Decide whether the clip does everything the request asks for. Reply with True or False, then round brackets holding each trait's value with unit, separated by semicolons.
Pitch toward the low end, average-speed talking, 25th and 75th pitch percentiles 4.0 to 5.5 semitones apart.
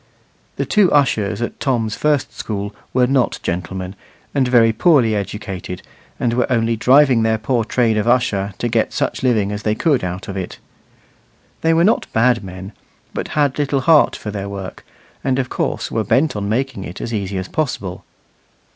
True (115 Hz; 180 wpm; 4.6 semitones)